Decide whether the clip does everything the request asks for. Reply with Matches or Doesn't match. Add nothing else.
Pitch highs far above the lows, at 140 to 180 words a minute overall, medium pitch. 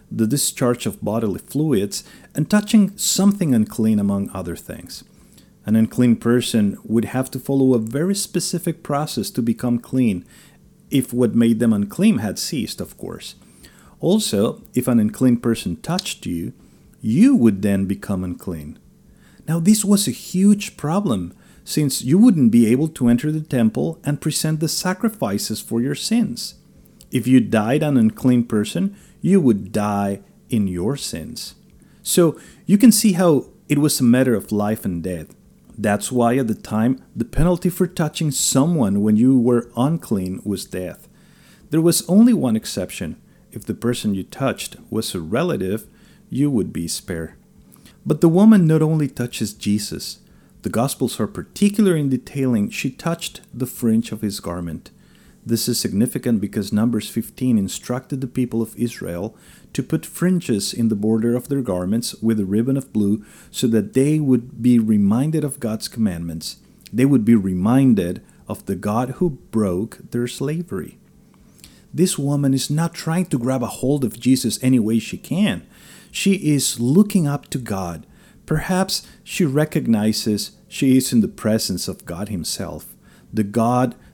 Doesn't match